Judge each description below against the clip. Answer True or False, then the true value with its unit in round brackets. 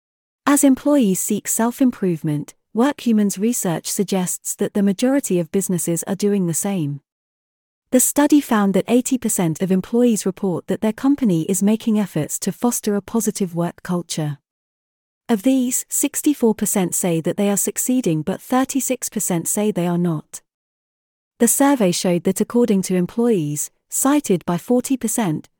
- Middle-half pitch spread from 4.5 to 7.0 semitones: True (5.2 semitones)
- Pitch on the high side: True (205 Hz)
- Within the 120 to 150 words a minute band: True (145 wpm)